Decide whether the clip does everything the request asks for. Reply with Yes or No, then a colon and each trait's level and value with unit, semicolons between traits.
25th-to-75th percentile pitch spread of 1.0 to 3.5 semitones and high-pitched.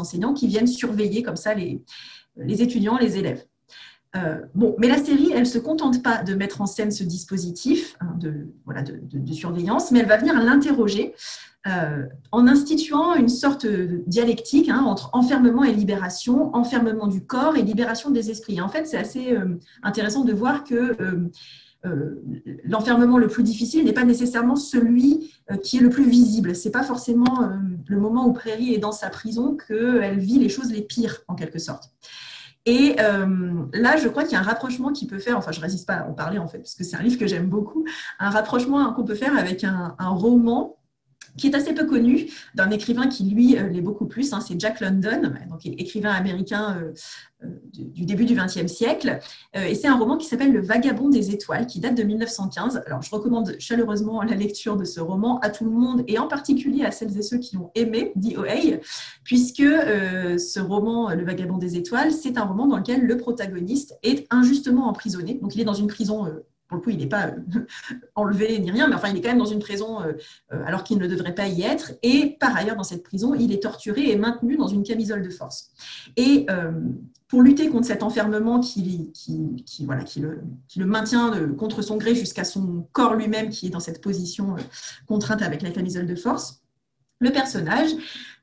No: average, 4.7 semitones; high, 220 Hz